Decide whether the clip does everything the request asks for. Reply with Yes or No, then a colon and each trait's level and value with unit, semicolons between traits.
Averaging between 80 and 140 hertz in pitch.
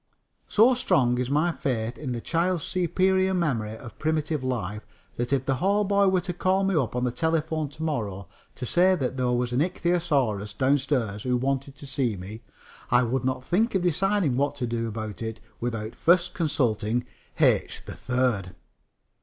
Yes: low, 135 Hz